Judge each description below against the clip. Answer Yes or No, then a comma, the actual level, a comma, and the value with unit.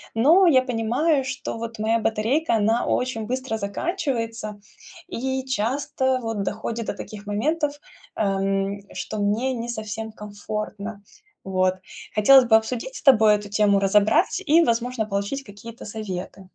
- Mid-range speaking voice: No, high, 225 Hz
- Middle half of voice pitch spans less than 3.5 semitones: No, average, 3.9 semitones